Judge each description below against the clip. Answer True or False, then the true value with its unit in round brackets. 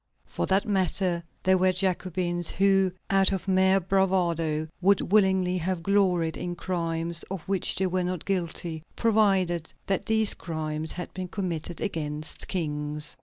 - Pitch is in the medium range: True (180 Hz)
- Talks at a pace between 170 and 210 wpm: False (145 wpm)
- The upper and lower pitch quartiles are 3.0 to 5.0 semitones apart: False (2.4 semitones)